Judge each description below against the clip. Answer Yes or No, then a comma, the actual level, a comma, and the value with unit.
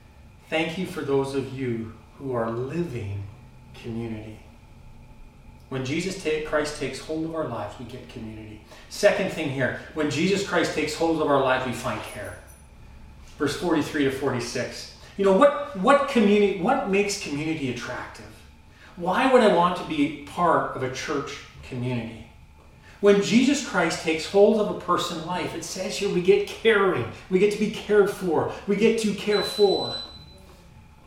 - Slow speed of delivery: No, average, 165 wpm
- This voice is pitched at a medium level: Yes, medium, 145 Hz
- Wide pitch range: Yes, wide, 8.2 semitones